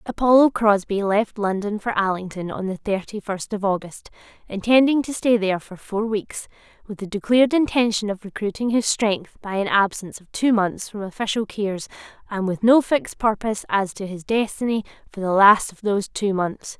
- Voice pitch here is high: Yes, high, 210 Hz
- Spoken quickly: No, average, 180 wpm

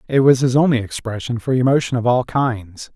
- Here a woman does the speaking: No, male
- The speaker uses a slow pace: No, fast, 205 wpm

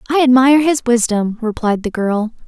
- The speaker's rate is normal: Yes, average, 170 wpm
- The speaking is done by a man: No, female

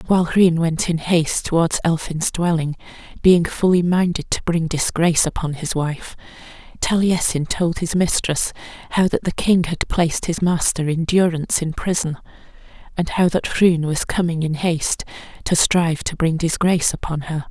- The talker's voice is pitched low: No, medium, 165 Hz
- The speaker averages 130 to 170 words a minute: Yes, average, 165 wpm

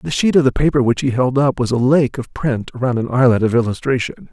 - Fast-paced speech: Yes, fast, 265 wpm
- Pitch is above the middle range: No, low, 130 Hz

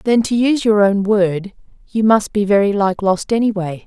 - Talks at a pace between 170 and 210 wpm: Yes, average, 200 wpm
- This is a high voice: Yes, high, 205 Hz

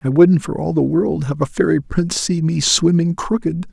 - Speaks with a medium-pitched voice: Yes, medium, 155 Hz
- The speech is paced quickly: Yes, fast, 225 wpm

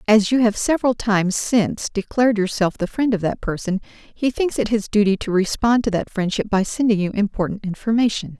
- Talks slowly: No, average, 200 wpm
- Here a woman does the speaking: Yes, female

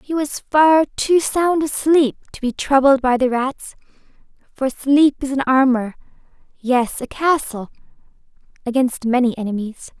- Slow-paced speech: Yes, slow, 125 wpm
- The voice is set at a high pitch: Yes, very high, 265 Hz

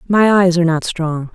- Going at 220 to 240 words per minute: Yes, fast, 225 wpm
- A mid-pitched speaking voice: Yes, medium, 175 Hz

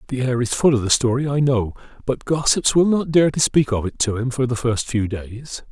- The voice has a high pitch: No, low, 125 Hz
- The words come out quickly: Yes, fast, 265 wpm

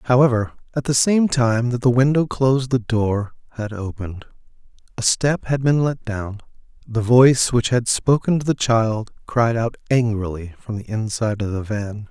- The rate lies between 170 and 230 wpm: Yes, average, 180 wpm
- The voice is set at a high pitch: No, low, 120 Hz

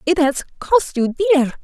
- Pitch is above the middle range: Yes, very high, 310 Hz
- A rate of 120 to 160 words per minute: No, average, 185 wpm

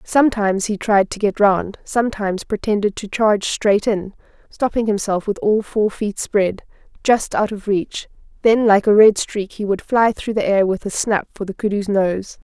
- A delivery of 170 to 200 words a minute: Yes, average, 190 wpm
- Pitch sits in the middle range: No, high, 205 Hz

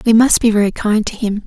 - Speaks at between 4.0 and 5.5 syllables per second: No, 5.9 syllables/s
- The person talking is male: No, female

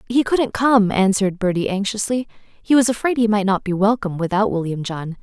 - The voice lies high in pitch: Yes, high, 210 Hz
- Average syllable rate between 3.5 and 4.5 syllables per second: No, 5.5 syllables/s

